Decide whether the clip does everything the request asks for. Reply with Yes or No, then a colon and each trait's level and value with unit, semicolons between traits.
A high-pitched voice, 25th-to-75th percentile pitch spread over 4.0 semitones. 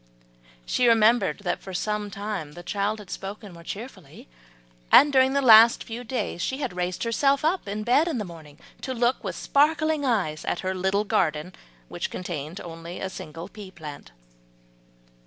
Yes: high, 205 Hz; wide, 5.4 semitones